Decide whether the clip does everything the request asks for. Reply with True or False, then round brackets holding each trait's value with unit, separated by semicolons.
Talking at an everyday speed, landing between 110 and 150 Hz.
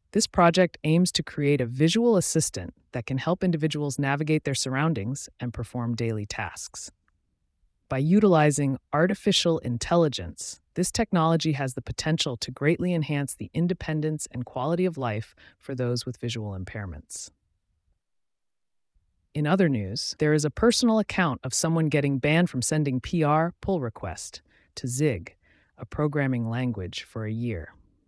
True (145 wpm; 140 Hz)